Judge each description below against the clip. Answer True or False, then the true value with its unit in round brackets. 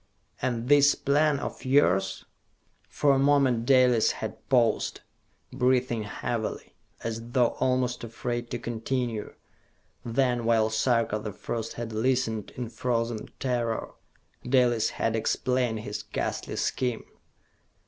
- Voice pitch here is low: True (120 Hz)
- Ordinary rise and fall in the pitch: False (2.3 semitones)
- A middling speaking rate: False (115 wpm)